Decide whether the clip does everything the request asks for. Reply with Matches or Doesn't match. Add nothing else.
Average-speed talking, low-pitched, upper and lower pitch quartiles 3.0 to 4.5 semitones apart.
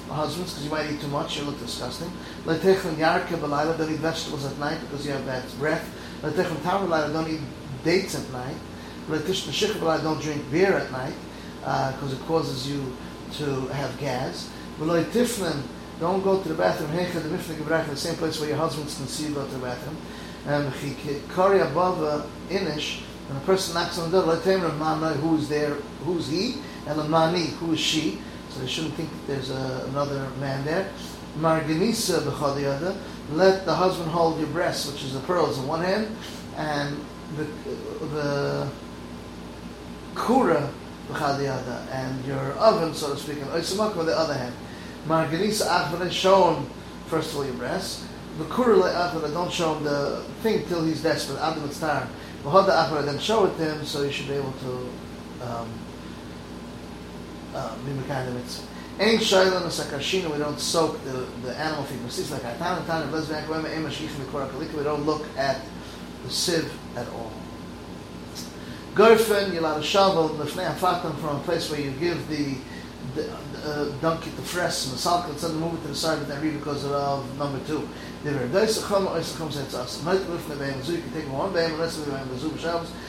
Doesn't match